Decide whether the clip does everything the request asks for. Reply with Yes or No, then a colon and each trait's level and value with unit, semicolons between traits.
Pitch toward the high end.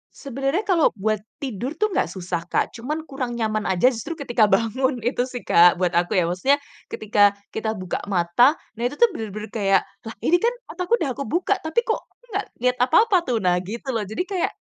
Yes: high, 240 Hz